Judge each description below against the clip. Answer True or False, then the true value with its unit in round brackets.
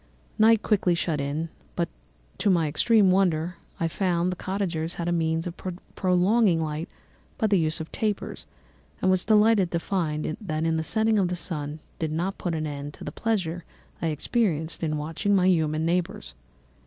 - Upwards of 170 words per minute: True (180 wpm)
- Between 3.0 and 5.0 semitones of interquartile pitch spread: True (3.4 semitones)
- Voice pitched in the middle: True (170 Hz)